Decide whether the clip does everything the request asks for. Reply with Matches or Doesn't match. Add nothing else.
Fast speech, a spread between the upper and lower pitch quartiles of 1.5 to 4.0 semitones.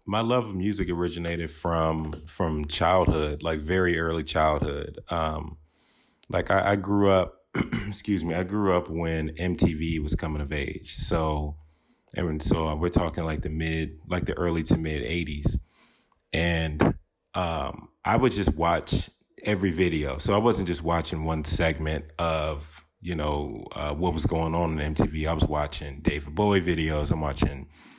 Doesn't match